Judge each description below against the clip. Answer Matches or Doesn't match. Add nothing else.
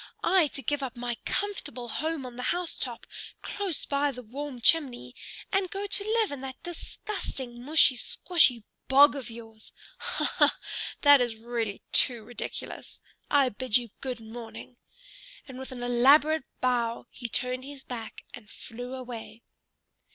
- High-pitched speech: Matches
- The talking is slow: Doesn't match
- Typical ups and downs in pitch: Matches